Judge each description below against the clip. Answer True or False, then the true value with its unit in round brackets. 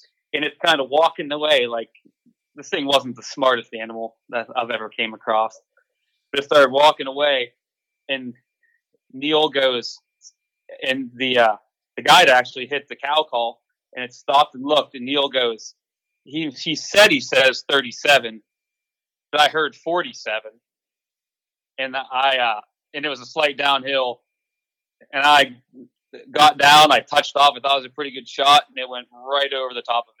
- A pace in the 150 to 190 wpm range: True (175 wpm)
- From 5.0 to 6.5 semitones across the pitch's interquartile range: False (3.3 semitones)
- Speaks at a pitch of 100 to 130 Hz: False (140 Hz)